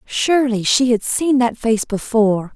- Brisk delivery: No, average, 165 wpm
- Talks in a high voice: Yes, high, 235 Hz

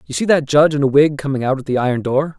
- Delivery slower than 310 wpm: No, fast, 325 wpm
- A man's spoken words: Yes, male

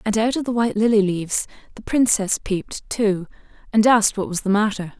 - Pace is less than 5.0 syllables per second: No, 5.5 syllables/s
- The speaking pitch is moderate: No, high, 210 Hz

